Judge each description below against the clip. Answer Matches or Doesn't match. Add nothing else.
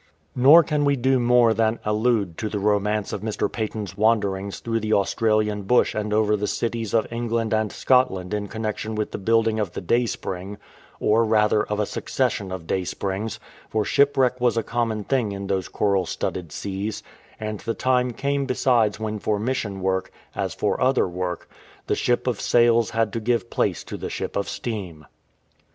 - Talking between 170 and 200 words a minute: Matches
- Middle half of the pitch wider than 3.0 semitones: Doesn't match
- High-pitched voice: Doesn't match